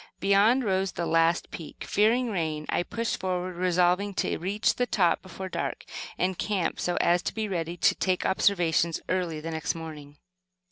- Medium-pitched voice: Yes, medium, 180 Hz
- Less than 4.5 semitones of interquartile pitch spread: Yes, average, 3.0 semitones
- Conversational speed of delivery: Yes, average, 175 wpm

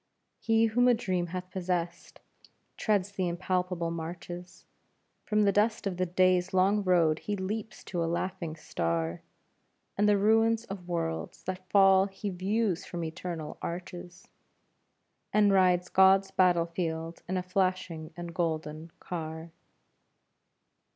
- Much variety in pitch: No, narrow, 2.5 semitones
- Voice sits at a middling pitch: Yes, medium, 180 Hz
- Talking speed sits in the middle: No, slow, 130 wpm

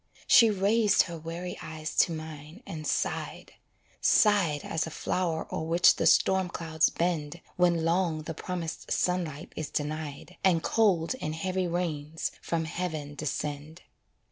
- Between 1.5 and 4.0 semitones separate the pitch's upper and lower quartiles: Yes, narrow, 2.5 semitones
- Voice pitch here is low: No, medium, 165 Hz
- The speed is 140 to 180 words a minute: Yes, average, 145 wpm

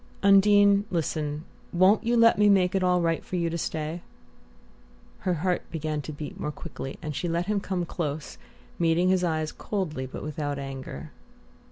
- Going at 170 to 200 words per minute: Yes, average, 175 wpm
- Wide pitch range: No, average, 3.8 semitones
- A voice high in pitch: No, medium, 170 Hz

